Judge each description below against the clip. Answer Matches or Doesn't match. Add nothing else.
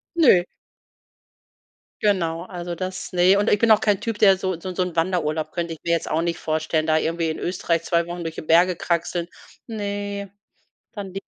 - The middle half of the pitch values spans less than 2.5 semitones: Doesn't match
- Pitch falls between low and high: Matches